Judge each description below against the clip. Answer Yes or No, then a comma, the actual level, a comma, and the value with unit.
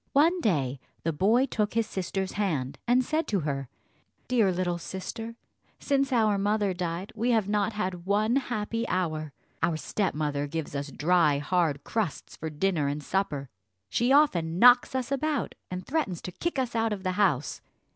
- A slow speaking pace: No, average, 170 wpm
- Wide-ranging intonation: Yes, wide, 6.0 semitones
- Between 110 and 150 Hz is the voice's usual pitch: No, high, 195 Hz